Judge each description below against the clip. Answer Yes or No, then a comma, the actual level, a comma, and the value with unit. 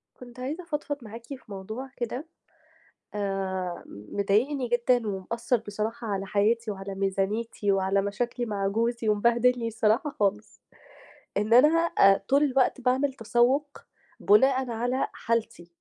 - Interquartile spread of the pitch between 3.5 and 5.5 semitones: Yes, average, 3.8 semitones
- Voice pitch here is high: Yes, high, 230 Hz